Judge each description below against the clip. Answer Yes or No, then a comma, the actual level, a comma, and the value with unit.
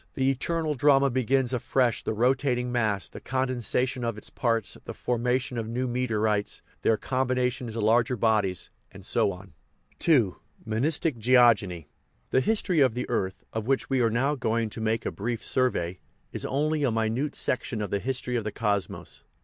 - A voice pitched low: Yes, low, 120 Hz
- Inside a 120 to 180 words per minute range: Yes, average, 175 wpm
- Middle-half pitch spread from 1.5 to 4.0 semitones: Yes, average, 3.0 semitones